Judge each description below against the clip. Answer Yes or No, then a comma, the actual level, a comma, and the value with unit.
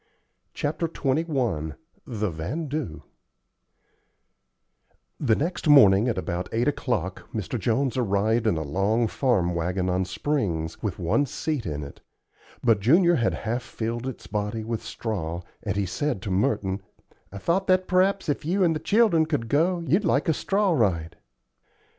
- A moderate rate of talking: Yes, average, 155 wpm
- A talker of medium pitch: No, low, 115 Hz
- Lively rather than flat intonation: Yes, wide, 7.9 semitones